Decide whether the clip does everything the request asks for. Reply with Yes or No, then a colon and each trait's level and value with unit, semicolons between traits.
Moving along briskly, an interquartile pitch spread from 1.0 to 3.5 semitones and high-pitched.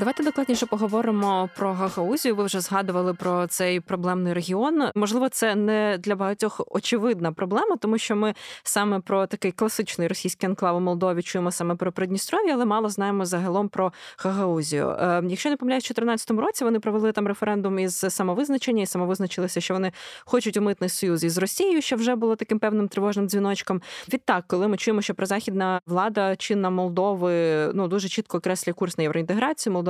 Yes: fast, 175 wpm; average, 3.1 semitones; high, 195 Hz